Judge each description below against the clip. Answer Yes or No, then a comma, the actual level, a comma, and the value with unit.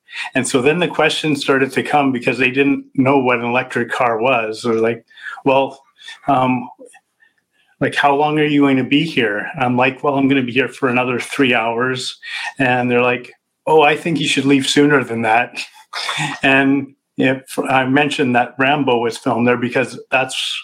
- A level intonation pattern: Yes, narrow, 2.2 semitones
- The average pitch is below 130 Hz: No, low, 135 Hz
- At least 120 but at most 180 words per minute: No, average, 195 wpm